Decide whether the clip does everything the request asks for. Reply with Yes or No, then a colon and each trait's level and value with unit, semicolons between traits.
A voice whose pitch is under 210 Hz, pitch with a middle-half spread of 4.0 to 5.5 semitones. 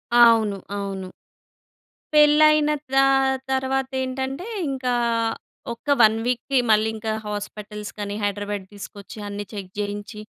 No: high, 215 Hz; average, 4.4 semitones